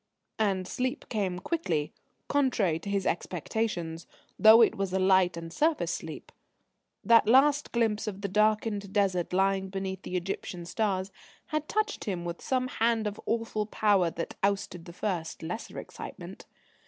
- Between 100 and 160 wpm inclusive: Yes, average, 155 wpm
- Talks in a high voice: Yes, high, 200 Hz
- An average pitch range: Yes, average, 3.7 semitones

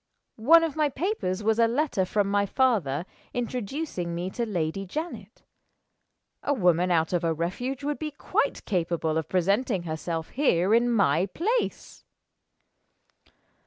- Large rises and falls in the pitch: Yes, wide, 7.3 semitones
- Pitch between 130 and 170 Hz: No, high, 200 Hz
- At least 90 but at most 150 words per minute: Yes, average, 140 wpm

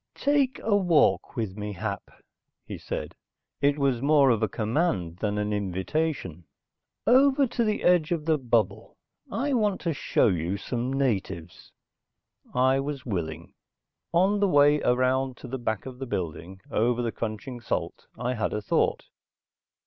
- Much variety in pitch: Yes, wide, 6.9 semitones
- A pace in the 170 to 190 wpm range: No, average, 155 wpm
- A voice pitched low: Yes, low, 125 Hz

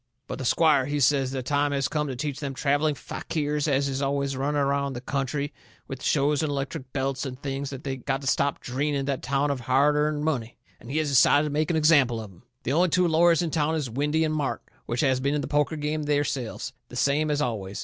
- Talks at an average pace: No, fast, 240 wpm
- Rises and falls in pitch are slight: Yes, narrow, 1.9 semitones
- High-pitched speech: No, medium, 140 Hz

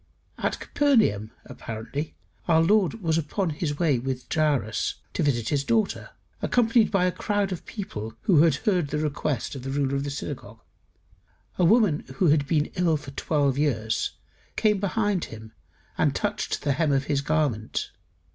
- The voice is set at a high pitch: No, medium, 150 Hz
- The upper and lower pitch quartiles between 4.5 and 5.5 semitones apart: Yes, average, 5.0 semitones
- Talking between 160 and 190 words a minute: Yes, average, 165 wpm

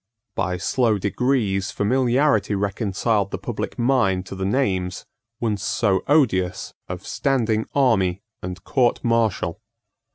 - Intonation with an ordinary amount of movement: Yes, average, 4.4 semitones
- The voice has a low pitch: Yes, low, 105 Hz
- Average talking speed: No, slow, 120 wpm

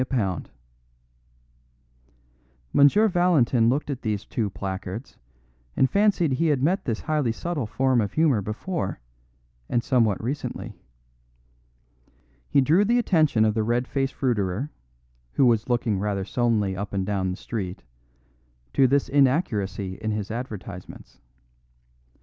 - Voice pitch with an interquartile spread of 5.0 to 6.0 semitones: Yes, wide, 5.6 semitones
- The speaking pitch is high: No, low, 120 Hz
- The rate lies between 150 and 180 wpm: No, slow, 135 wpm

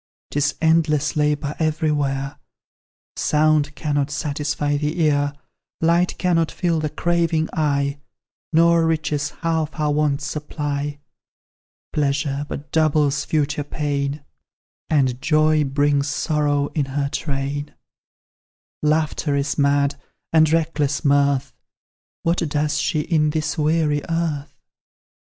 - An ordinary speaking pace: No, slow, 110 wpm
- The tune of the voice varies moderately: No, narrow, 1.6 semitones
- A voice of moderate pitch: Yes, medium, 150 Hz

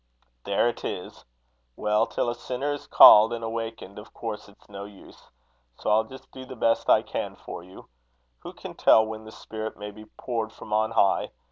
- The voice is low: Yes, low, 110 Hz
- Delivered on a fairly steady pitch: Yes, narrow, 1.6 semitones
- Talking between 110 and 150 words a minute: No, average, 200 wpm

